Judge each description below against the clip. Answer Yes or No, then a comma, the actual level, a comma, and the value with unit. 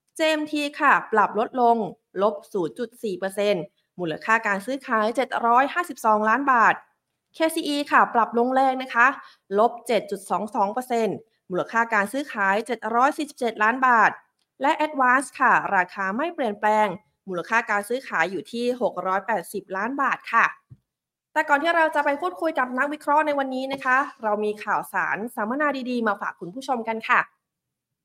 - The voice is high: Yes, high, 235 Hz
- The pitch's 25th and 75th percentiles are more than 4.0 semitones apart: Yes, average, 4.7 semitones